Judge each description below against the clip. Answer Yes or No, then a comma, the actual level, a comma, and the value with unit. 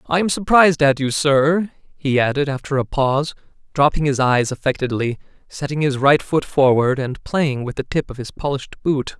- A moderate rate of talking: Yes, average, 190 wpm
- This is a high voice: No, medium, 140 Hz